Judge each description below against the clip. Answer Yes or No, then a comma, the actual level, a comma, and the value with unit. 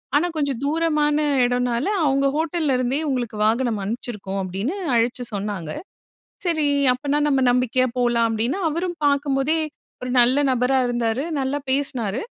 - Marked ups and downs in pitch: No, average, 3.5 semitones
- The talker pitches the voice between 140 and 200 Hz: No, very high, 255 Hz